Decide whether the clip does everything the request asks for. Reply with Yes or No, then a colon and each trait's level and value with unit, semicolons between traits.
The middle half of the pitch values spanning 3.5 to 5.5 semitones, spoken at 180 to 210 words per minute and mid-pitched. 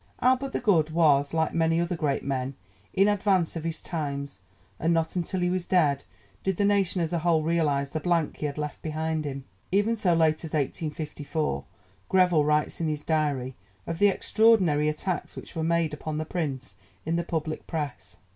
No: average, 2.7 semitones; average, 190 wpm; medium, 160 Hz